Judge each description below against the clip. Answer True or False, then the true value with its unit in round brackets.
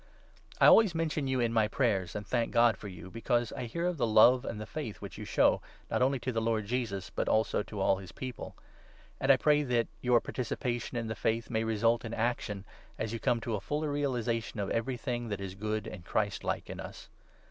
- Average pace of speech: False (235 wpm)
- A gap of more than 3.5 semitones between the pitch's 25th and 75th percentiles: False (2.8 semitones)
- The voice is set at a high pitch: False (115 Hz)